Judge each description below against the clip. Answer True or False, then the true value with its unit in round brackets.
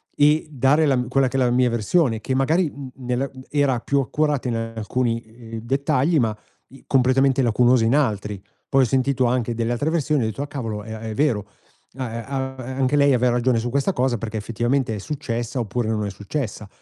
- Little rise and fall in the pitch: False (3.1 semitones)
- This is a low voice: True (125 Hz)